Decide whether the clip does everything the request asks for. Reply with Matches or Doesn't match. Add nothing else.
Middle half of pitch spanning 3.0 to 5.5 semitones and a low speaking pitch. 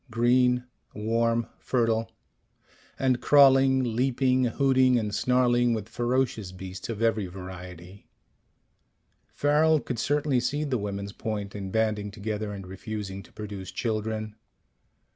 Matches